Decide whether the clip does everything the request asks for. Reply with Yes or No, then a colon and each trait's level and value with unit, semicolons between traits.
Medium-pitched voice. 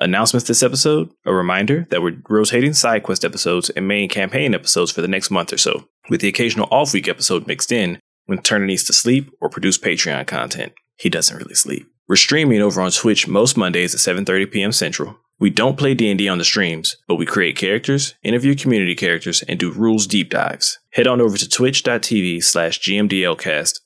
No: low, 105 Hz